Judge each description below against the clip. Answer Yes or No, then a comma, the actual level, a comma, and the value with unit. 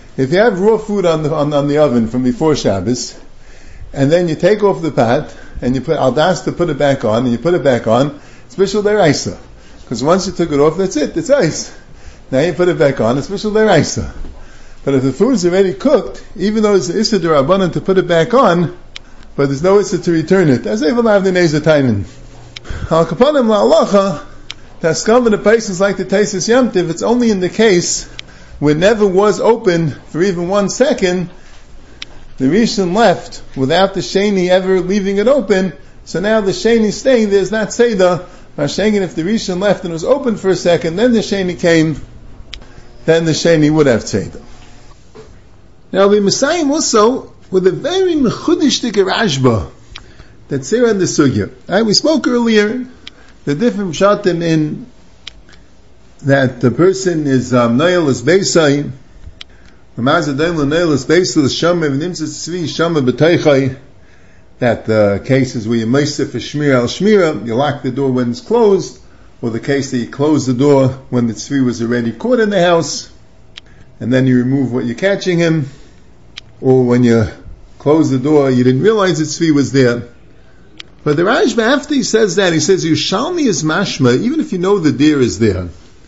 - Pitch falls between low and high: Yes, medium, 160 Hz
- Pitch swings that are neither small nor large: No, wide, 7.3 semitones